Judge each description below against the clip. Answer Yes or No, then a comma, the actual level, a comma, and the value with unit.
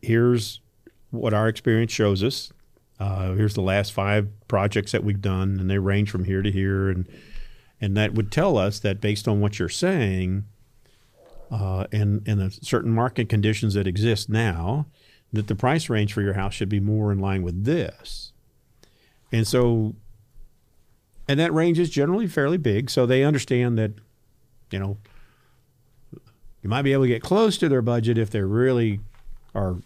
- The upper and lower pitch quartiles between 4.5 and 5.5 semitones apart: No, average, 3.6 semitones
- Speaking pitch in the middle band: No, low, 110 Hz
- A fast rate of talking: No, average, 175 wpm